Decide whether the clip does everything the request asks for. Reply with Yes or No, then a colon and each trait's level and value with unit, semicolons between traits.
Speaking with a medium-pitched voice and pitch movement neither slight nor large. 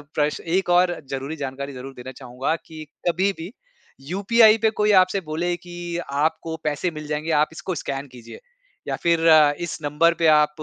Yes: medium, 160 Hz; average, 3.6 semitones